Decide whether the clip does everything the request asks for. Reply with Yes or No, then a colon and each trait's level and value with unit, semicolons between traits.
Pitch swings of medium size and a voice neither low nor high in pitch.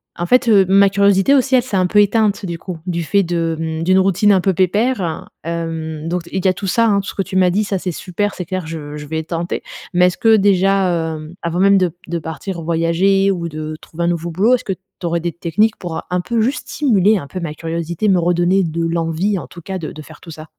Yes: average, 3.0 semitones; medium, 180 Hz